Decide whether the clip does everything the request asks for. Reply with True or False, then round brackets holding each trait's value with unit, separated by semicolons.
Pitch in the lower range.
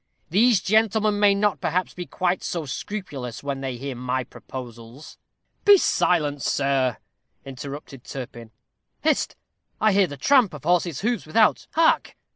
False (155 Hz)